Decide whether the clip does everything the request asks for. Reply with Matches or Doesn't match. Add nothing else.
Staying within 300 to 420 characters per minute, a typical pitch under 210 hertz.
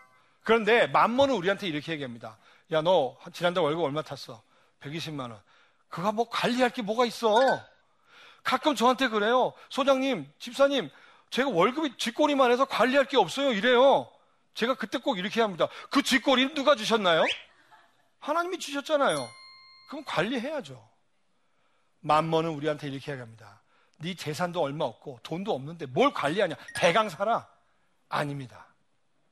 Doesn't match